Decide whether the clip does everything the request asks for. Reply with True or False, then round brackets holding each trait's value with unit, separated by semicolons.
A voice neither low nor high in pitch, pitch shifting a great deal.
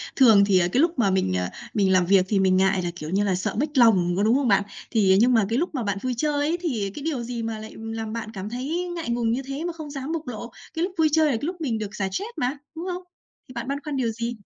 False (235 Hz; 6.2 semitones)